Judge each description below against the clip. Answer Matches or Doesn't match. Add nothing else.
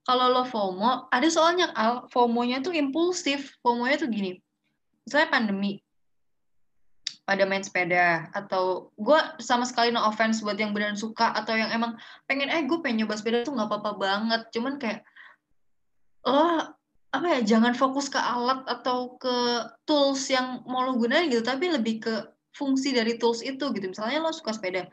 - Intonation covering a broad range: Doesn't match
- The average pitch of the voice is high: Matches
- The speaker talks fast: Matches